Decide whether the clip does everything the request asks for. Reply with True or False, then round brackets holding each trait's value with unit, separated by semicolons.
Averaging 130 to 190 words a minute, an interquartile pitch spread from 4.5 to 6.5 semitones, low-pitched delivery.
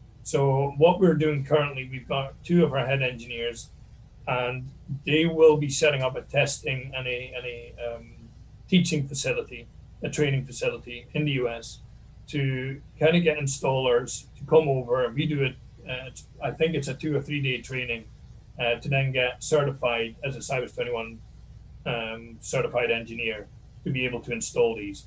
False (170 wpm; 3.5 semitones; 130 Hz)